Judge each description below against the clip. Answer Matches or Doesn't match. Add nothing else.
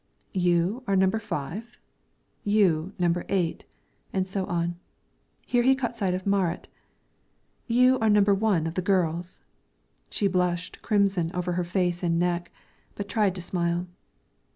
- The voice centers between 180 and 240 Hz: Matches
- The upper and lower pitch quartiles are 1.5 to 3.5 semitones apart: Matches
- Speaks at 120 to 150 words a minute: Matches